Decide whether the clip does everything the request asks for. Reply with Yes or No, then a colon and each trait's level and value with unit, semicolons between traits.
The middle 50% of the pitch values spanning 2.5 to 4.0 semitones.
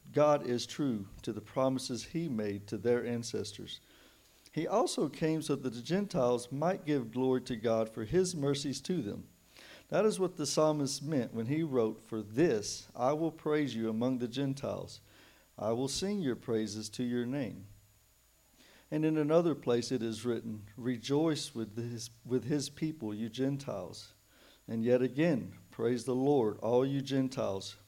No: average, 4.5 semitones